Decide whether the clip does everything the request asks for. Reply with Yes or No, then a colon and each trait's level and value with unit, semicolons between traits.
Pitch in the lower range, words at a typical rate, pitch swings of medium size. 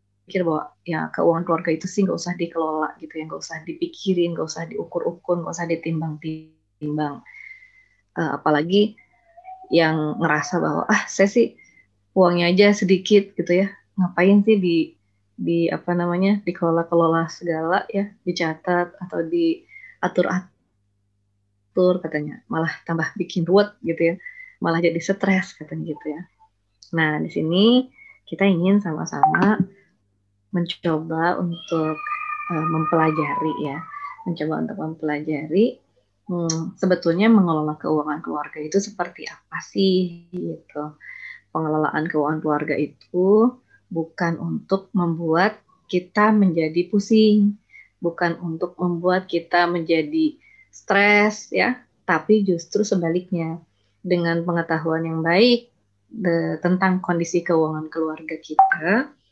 No: medium, 175 Hz; average, 120 wpm; average, 3.7 semitones